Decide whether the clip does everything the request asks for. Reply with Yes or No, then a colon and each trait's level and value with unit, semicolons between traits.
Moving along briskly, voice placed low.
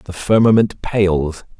No: slow, 115 wpm; very low, 95 Hz